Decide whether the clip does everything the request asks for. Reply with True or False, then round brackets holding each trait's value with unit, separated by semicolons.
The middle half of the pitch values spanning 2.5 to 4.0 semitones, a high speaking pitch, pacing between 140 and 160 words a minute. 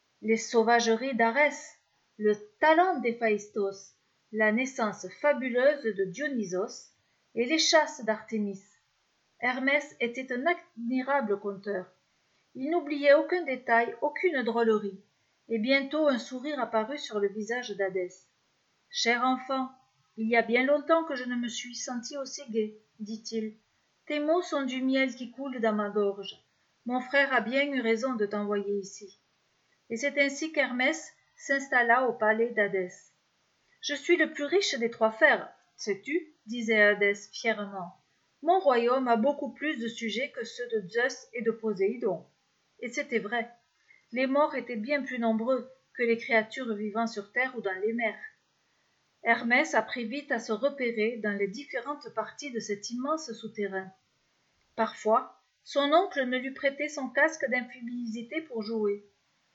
False (4.4 semitones; 240 Hz; 150 wpm)